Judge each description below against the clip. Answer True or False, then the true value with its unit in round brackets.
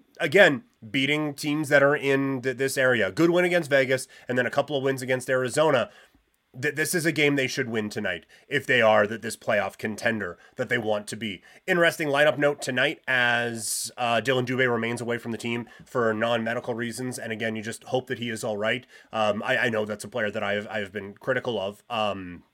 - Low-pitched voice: True (125 Hz)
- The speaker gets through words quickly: True (225 wpm)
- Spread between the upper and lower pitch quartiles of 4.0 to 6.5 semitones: False (3.6 semitones)